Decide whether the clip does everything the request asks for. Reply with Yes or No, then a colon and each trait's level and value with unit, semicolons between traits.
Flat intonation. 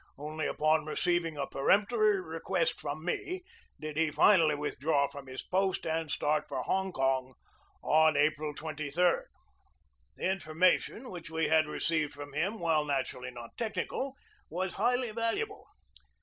No: average, 4.2 semitones